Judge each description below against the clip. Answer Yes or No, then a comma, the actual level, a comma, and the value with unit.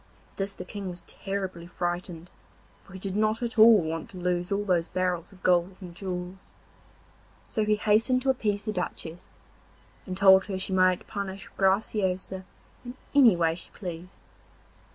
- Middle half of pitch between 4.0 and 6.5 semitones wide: No, narrow, 2.5 semitones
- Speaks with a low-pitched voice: No, high, 190 Hz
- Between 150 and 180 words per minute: Yes, average, 170 wpm